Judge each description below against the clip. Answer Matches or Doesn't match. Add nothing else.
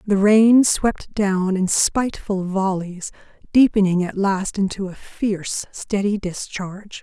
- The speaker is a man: Doesn't match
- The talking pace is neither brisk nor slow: Doesn't match